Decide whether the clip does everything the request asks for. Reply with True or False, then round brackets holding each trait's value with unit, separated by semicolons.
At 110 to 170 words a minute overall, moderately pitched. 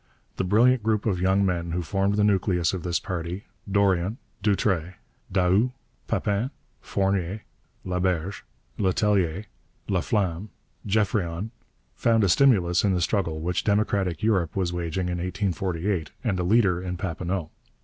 False (135 wpm; 95 Hz)